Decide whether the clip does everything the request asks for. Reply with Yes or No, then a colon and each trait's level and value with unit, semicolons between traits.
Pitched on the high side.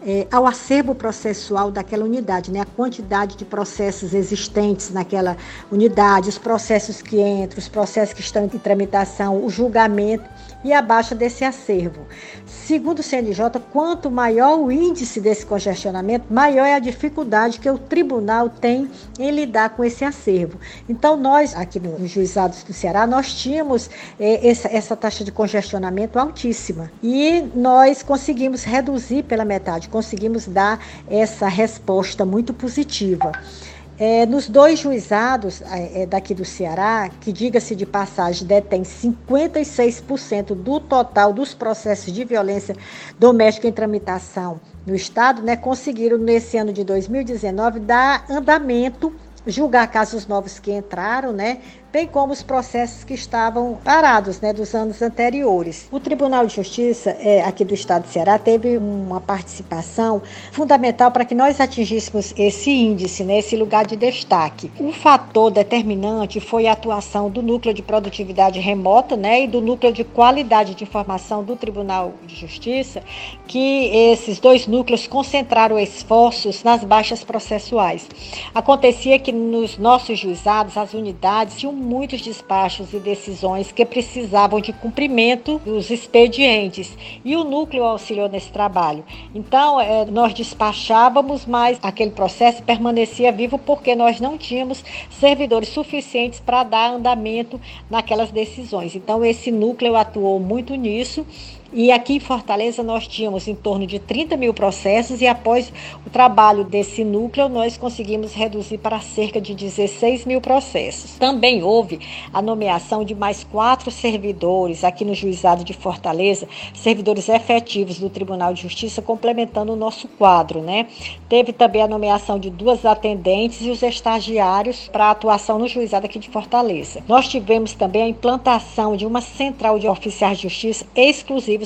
Yes: high, 225 Hz